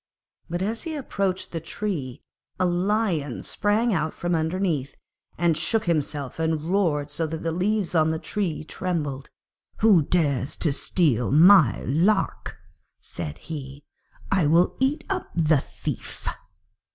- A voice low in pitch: No, medium, 165 Hz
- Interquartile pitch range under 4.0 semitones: No, average, 4.7 semitones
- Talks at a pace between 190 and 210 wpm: No, average, 140 wpm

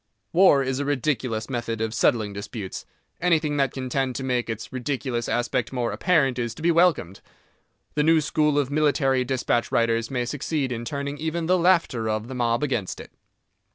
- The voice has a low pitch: Yes, low, 130 Hz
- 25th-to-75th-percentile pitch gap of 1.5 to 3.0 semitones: No, average, 4.0 semitones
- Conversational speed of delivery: Yes, average, 185 wpm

